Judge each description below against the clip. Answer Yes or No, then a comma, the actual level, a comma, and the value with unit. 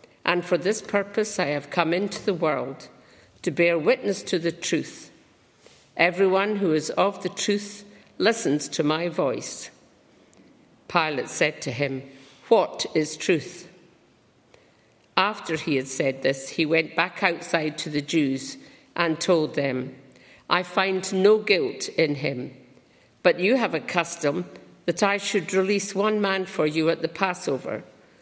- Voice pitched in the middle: Yes, medium, 175 Hz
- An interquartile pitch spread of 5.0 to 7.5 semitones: No, average, 4.1 semitones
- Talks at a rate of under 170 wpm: Yes, average, 150 wpm